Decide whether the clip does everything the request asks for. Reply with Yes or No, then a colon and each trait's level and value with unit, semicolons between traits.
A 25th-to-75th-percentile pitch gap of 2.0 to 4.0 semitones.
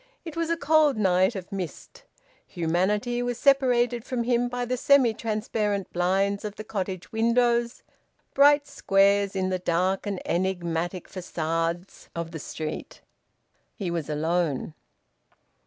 No: wide, 5.4 semitones